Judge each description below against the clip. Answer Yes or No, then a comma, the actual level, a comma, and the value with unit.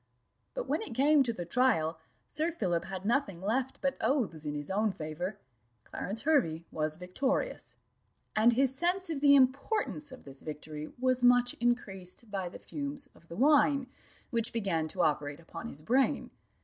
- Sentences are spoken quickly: No, average, 170 wpm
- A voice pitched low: No, high, 230 Hz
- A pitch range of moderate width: No, wide, 8.2 semitones